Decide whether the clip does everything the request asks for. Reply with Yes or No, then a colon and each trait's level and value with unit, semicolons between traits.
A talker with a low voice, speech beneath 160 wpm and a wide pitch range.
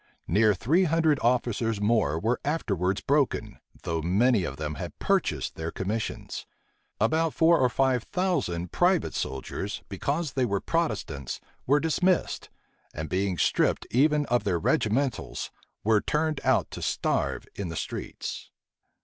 Yes: low, 115 Hz; average, 140 wpm; wide, 7.7 semitones